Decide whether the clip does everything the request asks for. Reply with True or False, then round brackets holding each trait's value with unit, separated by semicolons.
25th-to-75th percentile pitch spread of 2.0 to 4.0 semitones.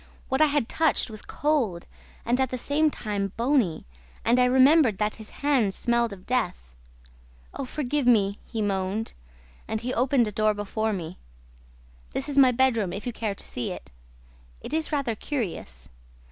False (4.5 semitones)